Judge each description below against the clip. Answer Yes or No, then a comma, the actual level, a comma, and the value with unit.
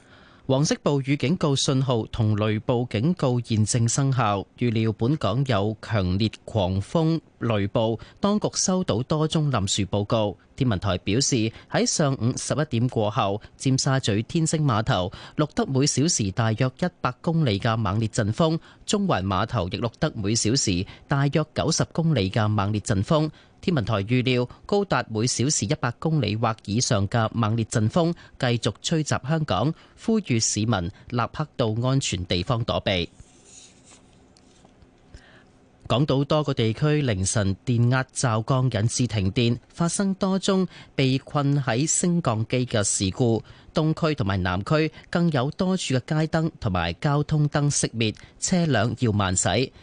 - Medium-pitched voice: No, low, 125 Hz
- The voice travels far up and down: Yes, wide, 5.8 semitones